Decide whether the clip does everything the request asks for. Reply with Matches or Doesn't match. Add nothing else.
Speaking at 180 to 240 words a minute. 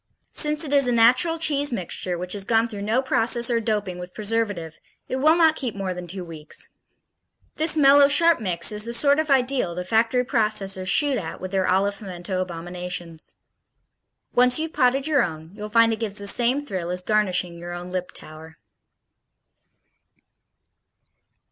Doesn't match